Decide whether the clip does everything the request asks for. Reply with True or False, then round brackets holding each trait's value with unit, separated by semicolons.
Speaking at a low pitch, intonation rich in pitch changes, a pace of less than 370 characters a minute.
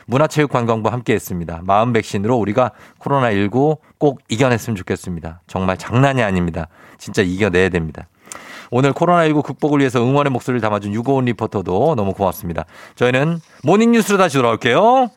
False (120 Hz; 6.2 semitones; 410 characters per minute)